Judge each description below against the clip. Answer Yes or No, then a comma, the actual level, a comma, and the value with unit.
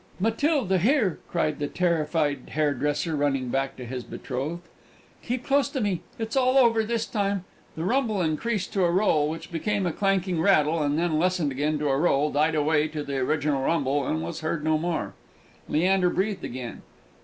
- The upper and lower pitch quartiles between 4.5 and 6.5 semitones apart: Yes, average, 5.0 semitones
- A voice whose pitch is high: No, medium, 165 Hz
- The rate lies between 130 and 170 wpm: No, average, 180 wpm